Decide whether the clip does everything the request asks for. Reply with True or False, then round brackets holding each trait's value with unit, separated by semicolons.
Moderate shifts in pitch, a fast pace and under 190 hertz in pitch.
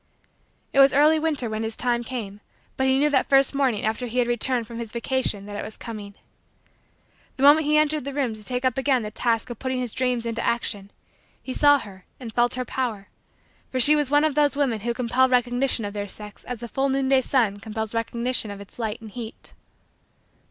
False (3.3 semitones; 220 wpm; 245 Hz)